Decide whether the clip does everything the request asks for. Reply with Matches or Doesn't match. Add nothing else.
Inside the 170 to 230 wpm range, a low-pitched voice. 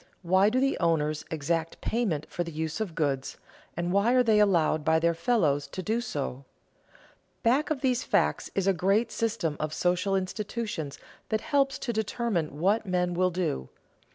Doesn't match